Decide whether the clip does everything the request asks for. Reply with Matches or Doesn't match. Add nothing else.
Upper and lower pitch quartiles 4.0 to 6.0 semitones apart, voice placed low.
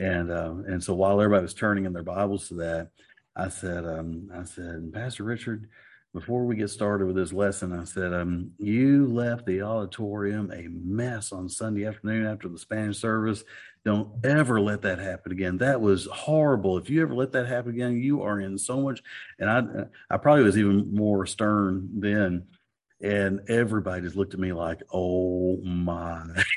Doesn't match